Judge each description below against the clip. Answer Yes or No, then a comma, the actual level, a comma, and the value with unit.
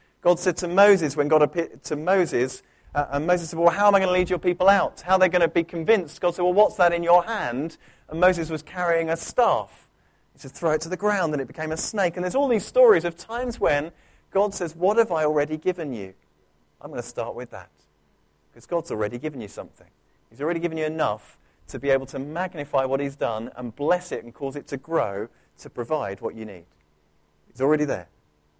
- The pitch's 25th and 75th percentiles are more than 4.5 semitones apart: Yes, average, 5.0 semitones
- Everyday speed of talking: No, fast, 235 wpm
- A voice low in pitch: No, medium, 160 Hz